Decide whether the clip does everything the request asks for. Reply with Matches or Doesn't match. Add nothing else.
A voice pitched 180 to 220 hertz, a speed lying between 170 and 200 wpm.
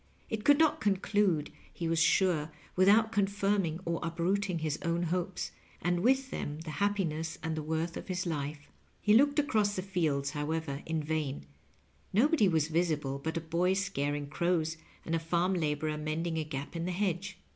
Doesn't match